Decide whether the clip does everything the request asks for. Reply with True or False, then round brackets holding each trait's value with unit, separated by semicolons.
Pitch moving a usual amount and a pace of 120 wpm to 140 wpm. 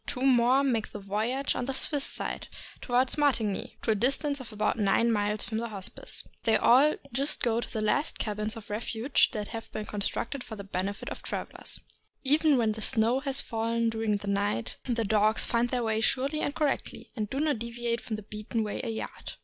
False (3.4 semitones; 205 wpm)